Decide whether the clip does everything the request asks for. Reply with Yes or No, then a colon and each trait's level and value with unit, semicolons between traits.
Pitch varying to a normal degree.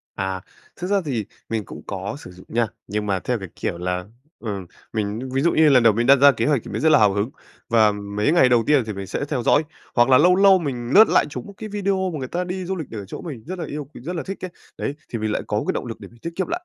No: wide, 7.9 semitones